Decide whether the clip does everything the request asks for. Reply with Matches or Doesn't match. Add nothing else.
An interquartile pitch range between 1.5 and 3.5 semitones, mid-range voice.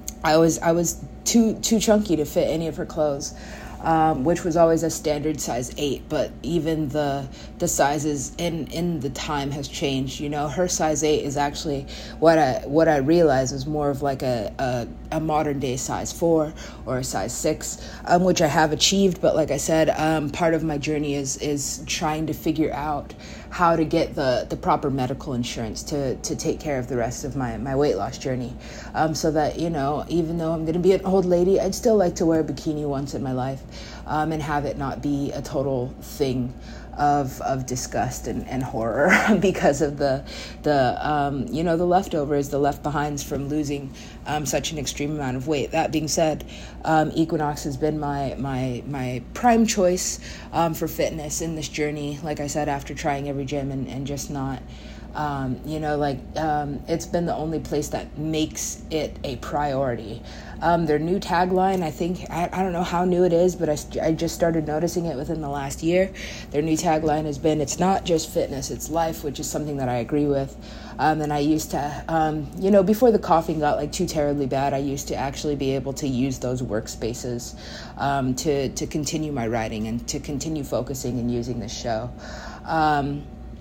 Matches